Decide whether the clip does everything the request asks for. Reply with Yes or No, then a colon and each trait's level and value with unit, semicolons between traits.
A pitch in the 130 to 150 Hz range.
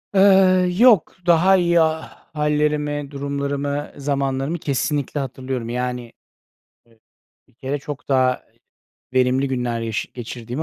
Yes: medium, 140 Hz